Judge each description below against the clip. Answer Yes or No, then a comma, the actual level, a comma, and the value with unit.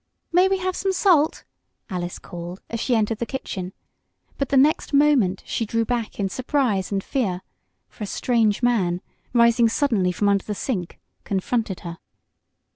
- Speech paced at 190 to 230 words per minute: No, average, 165 wpm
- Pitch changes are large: Yes, wide, 5.7 semitones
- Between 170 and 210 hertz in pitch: No, high, 225 Hz